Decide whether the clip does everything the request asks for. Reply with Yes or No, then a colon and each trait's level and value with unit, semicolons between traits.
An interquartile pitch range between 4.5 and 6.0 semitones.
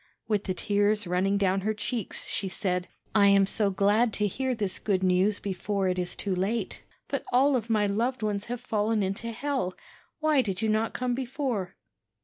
No: average, 3.2 semitones